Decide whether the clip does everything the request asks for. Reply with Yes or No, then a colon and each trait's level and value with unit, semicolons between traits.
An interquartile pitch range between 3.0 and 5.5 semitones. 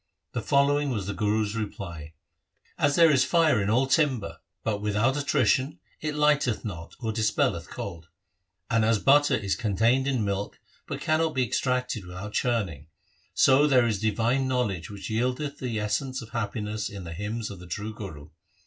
Yes: average, 4.6 semitones